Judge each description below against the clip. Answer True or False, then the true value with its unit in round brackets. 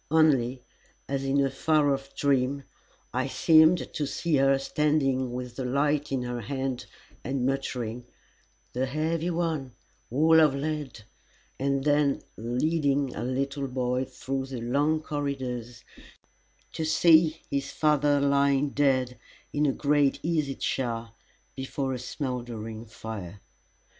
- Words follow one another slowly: True (130 wpm)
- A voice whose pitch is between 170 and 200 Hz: False (135 Hz)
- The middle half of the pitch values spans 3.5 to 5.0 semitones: False (2.7 semitones)